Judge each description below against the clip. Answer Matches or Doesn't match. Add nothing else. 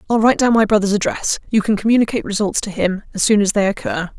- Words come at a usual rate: Doesn't match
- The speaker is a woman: Matches